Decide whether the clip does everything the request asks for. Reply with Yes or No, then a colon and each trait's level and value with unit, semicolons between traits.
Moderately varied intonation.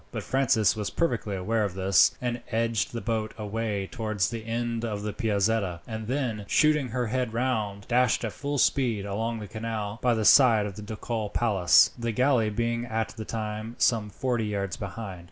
No: narrow, 2.3 semitones